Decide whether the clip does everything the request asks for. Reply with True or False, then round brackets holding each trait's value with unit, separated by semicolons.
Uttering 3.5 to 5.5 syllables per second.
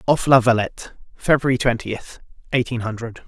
True (5.3 syllables/s)